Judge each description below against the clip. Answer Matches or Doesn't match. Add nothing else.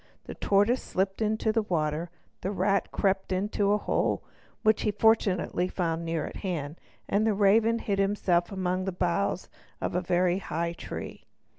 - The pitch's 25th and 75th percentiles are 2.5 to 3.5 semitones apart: Matches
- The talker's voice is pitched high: Matches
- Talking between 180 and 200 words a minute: Doesn't match